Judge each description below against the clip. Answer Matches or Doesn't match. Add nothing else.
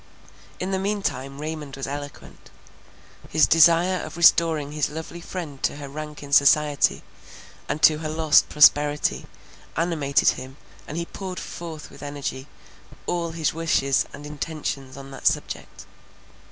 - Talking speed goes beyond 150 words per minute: Doesn't match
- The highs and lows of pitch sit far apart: Doesn't match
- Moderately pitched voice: Matches